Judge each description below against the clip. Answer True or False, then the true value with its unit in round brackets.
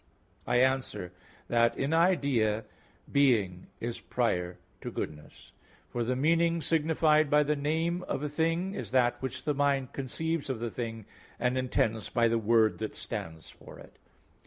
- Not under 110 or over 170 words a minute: True (160 wpm)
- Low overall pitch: True (130 Hz)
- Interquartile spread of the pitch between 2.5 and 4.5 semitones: False (4.9 semitones)